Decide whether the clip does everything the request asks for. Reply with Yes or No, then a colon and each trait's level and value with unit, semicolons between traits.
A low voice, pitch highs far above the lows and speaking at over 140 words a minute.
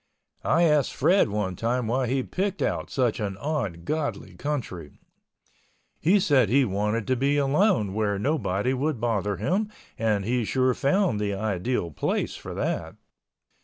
Yes: low, 125 Hz; wide, 5.8 semitones; average, 150 wpm